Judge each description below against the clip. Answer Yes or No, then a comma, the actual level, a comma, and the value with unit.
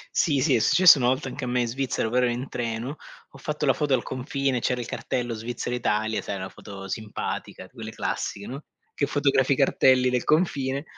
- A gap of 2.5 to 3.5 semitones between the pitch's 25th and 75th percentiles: Yes, average, 2.8 semitones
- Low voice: Yes, low, 125 Hz